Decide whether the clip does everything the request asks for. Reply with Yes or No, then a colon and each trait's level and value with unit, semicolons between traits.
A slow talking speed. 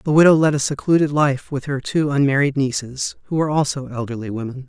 No: fast, 205 wpm